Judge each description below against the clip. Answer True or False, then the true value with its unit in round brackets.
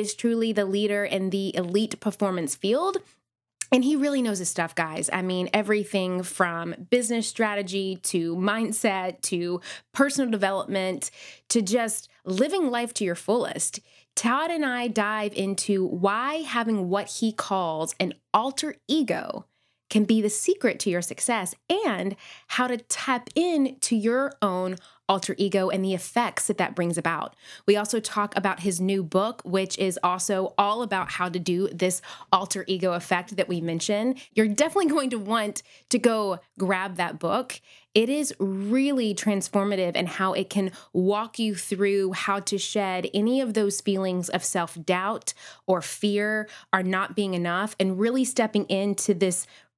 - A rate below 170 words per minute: True (160 wpm)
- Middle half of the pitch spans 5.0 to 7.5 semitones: False (3.4 semitones)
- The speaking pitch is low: False (200 Hz)